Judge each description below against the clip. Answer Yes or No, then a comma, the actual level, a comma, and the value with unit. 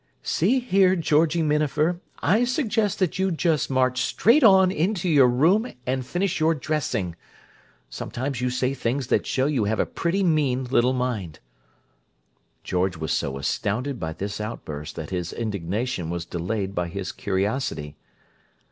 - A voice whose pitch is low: Yes, low, 130 Hz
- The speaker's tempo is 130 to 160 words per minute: Yes, average, 150 wpm